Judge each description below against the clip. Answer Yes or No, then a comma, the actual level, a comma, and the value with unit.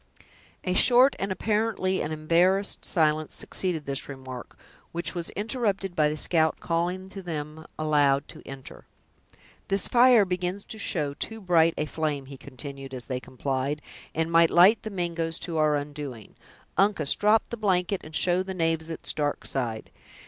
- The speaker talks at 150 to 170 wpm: Yes, average, 165 wpm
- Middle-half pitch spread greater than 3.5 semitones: Yes, average, 4.3 semitones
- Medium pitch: Yes, medium, 165 Hz